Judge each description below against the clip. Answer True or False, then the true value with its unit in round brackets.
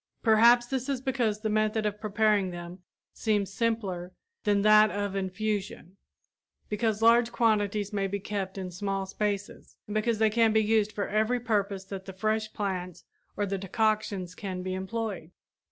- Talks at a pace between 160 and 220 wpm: True (165 wpm)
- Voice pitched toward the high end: True (210 Hz)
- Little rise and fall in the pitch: True (2.1 semitones)